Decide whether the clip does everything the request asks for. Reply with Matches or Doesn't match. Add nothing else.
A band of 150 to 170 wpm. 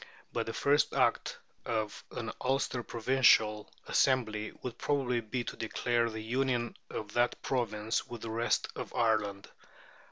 Doesn't match